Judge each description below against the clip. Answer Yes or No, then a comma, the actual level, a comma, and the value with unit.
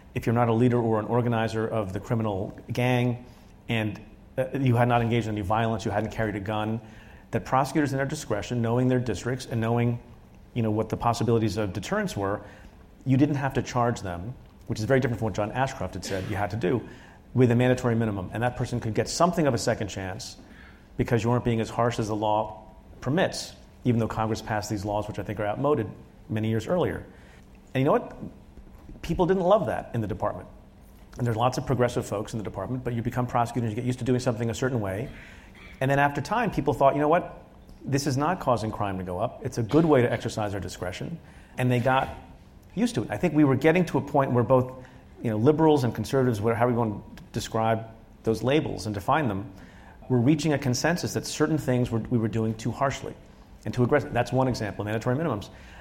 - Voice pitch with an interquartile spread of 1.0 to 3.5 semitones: Yes, average, 3.2 semitones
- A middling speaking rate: No, fast, 230 wpm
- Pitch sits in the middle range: No, low, 120 Hz